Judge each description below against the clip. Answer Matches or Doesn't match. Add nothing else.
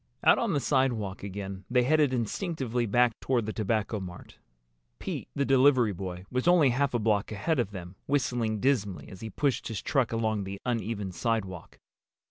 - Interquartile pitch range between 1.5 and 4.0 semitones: Doesn't match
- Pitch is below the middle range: Matches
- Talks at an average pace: Matches